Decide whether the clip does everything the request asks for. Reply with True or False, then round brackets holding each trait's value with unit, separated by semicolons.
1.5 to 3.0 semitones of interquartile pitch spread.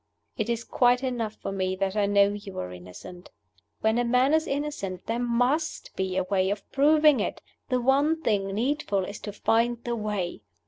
False (4.6 semitones)